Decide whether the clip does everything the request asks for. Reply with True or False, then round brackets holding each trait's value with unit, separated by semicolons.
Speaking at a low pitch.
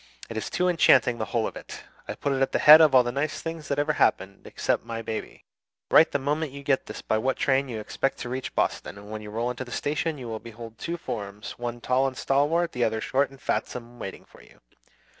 True (130 Hz)